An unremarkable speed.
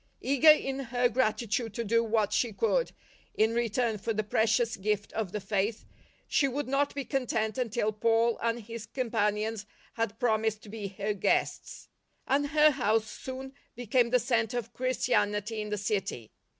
Yes: average, 170 wpm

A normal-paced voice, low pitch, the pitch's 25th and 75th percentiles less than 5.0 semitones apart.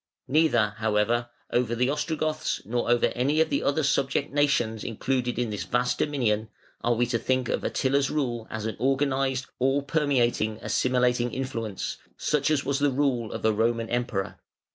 Yes: average, 165 wpm; low, 125 Hz; average, 3.2 semitones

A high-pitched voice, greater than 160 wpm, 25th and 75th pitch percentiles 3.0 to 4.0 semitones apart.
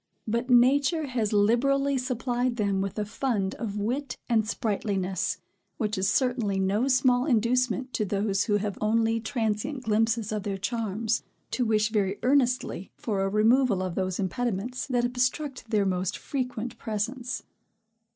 No: high, 225 Hz; average, 150 wpm; average, 3.5 semitones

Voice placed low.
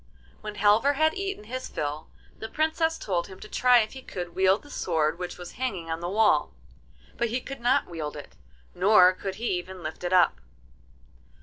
No: high, 195 Hz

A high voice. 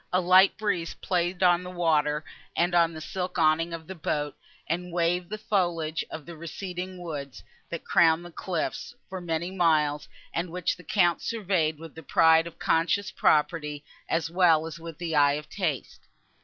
No: medium, 170 Hz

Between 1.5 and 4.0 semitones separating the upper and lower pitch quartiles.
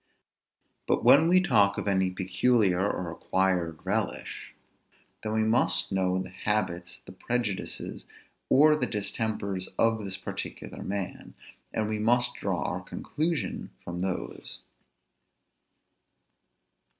Yes: average, 3.4 semitones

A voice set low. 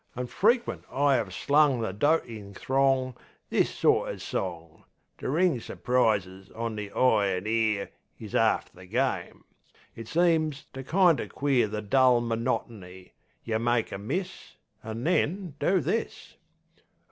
Yes: low, 120 Hz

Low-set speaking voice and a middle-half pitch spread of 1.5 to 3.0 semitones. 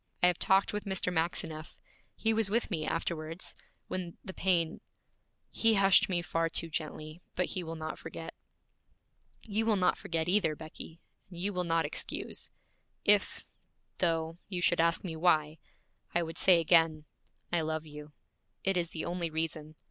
No: medium, 170 Hz; narrow, 2.5 semitones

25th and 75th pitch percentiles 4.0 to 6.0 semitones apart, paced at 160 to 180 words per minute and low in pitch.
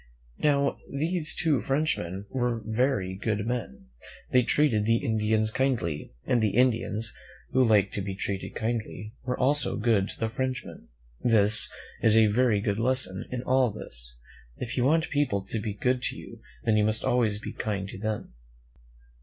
No: average, 3.6 semitones; average, 170 wpm; low, 115 Hz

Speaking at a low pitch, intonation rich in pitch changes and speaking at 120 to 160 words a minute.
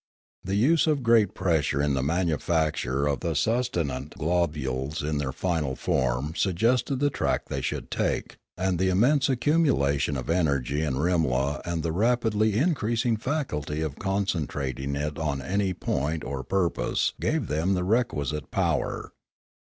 Yes: very low, 85 Hz; wide, 6.9 semitones; average, 145 wpm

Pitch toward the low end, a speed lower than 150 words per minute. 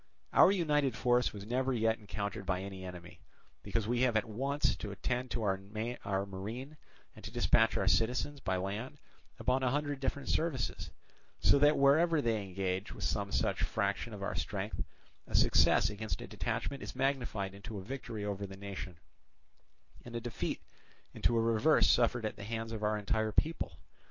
No: low, 115 Hz; average, 175 wpm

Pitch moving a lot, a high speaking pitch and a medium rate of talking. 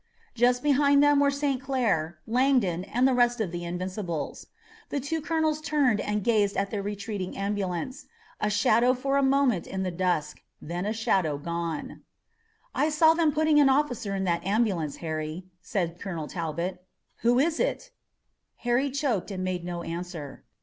Yes: wide, 7.3 semitones; high, 210 Hz; average, 170 wpm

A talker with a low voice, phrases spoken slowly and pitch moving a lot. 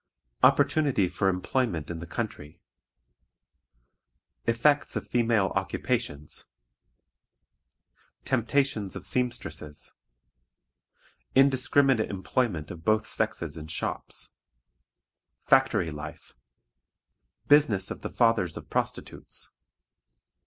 Yes: low, 110 Hz; slow, 80 wpm; wide, 7.0 semitones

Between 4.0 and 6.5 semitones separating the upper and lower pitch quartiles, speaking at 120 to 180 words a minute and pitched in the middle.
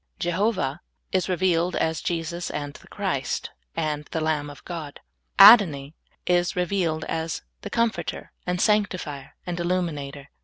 No: average, 3.5 semitones; average, 140 wpm; medium, 170 Hz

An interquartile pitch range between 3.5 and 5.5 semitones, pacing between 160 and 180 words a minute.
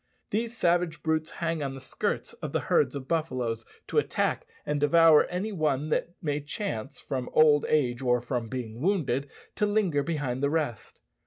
Yes: average, 4.4 semitones; average, 175 wpm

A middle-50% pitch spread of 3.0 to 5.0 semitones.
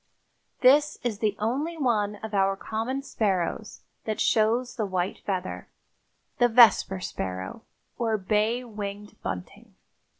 Yes: average, 3.6 semitones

